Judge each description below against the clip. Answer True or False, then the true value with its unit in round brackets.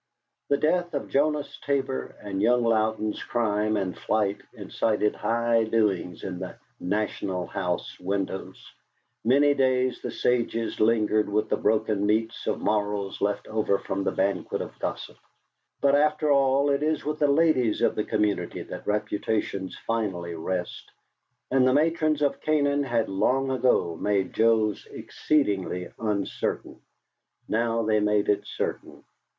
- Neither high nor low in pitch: False (110 Hz)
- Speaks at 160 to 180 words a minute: False (140 wpm)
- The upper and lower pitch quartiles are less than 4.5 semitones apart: False (4.8 semitones)